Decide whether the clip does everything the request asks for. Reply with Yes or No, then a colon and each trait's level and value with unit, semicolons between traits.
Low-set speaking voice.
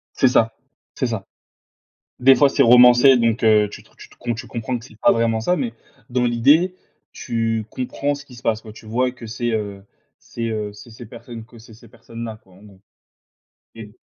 Yes: low, 115 Hz